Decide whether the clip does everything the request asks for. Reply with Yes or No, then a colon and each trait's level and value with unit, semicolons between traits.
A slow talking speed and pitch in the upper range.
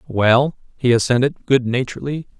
No: slow, 125 wpm; low, 130 Hz